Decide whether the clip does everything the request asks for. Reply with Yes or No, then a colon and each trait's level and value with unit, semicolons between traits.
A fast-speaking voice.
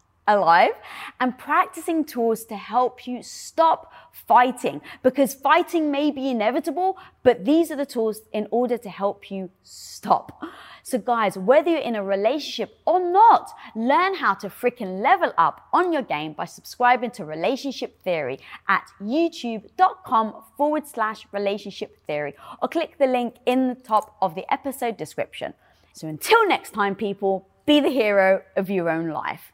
No: average, 155 wpm